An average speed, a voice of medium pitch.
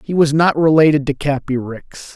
Yes: average, 195 wpm; medium, 145 Hz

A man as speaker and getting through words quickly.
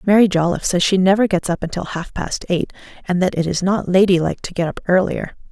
No: female; fast, 240 wpm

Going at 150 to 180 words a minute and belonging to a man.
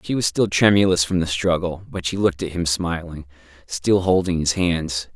No: average, 200 wpm; male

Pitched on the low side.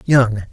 Yes: low, 120 Hz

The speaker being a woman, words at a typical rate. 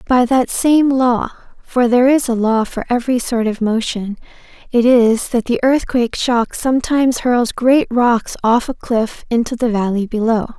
Yes: female; average, 175 wpm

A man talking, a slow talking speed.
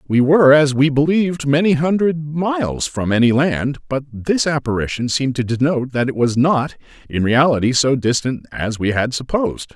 No: male; average, 180 wpm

